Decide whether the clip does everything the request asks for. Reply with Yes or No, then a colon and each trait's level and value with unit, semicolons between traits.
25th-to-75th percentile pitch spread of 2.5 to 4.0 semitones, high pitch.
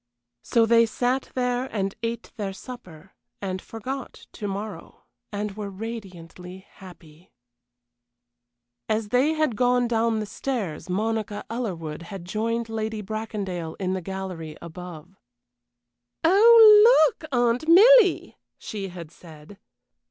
No: average, 4.8 semitones; high, 215 Hz